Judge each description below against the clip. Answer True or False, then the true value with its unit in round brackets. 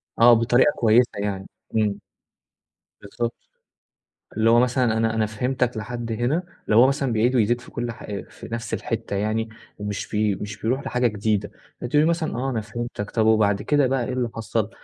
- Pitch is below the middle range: True (115 Hz)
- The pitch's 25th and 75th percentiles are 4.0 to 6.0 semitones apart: False (2.4 semitones)